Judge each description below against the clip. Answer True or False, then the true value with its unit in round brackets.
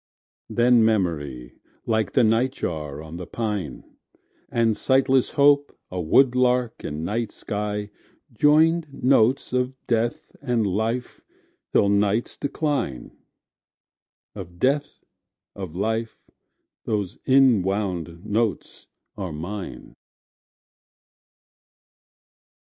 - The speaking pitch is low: True (110 Hz)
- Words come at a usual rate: False (90 wpm)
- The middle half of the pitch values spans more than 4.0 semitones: True (5.3 semitones)